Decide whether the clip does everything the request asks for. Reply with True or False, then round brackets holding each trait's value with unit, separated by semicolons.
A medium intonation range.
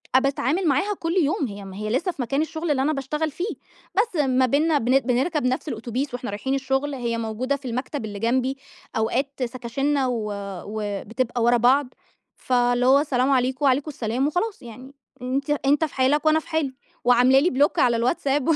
True (3.1 semitones)